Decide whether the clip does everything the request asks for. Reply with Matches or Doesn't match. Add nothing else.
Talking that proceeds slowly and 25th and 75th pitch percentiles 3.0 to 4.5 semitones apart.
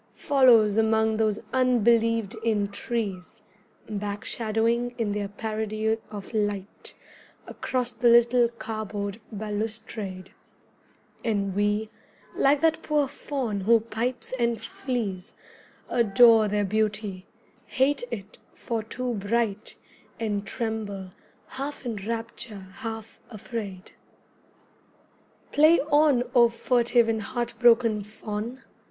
Doesn't match